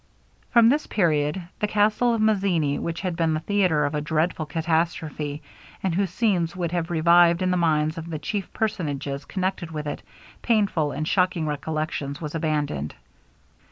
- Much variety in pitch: No, average, 3.6 semitones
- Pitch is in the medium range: Yes, medium, 165 Hz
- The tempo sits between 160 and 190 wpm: Yes, average, 165 wpm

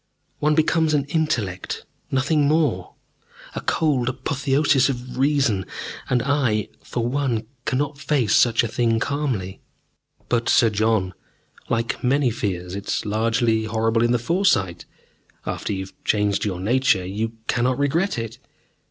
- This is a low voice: Yes, low, 120 Hz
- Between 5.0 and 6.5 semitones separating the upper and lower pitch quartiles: No, average, 4.5 semitones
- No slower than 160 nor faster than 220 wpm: No, average, 140 wpm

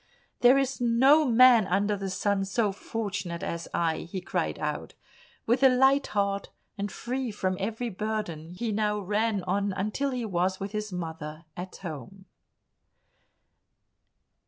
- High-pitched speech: Yes, high, 205 Hz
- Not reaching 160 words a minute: Yes, average, 145 wpm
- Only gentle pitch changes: No, average, 3.8 semitones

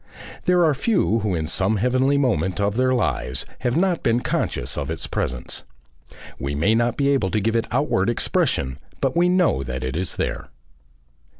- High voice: No, low, 115 Hz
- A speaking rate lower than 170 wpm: No, average, 185 wpm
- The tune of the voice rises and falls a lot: Yes, wide, 8.8 semitones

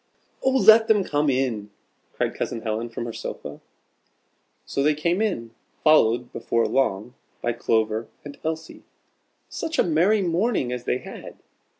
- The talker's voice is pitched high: No, medium, 140 Hz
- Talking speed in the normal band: Yes, average, 145 wpm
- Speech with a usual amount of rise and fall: No, wide, 7.3 semitones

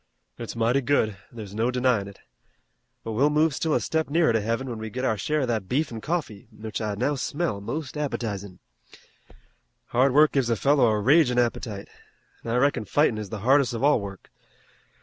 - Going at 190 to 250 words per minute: Yes, average, 200 wpm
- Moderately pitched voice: No, low, 120 Hz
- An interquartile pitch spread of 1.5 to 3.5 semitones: No, average, 4.8 semitones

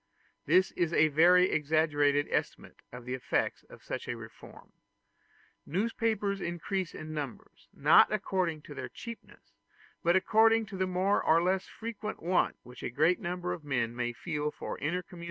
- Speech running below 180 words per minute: Yes, average, 170 wpm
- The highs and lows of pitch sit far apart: No, average, 4.2 semitones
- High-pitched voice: No, medium, 170 Hz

